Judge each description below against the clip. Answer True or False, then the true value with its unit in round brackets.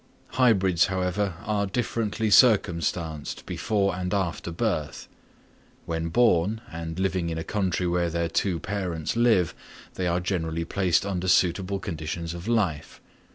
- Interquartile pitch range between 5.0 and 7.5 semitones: False (3.3 semitones)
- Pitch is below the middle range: True (90 Hz)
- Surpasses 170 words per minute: False (135 wpm)